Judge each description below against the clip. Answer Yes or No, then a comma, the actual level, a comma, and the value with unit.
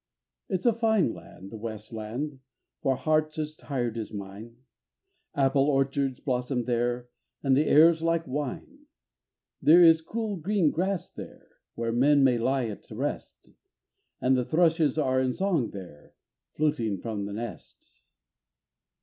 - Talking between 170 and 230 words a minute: No, average, 140 wpm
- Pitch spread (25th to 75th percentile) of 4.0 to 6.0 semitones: Yes, average, 5.2 semitones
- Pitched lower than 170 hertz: Yes, low, 135 Hz